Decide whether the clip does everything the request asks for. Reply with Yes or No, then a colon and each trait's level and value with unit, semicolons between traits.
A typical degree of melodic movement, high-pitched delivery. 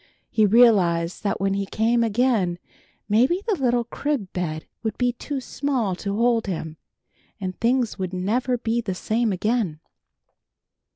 Yes: average, 4.4 semitones; high, 220 Hz